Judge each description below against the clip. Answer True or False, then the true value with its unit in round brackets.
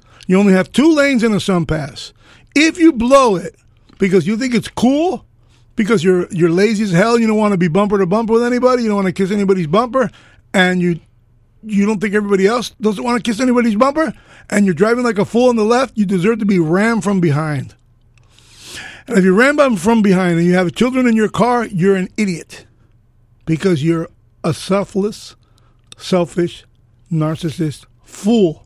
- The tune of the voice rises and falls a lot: True (6.2 semitones)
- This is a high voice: True (195 Hz)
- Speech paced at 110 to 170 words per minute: False (195 wpm)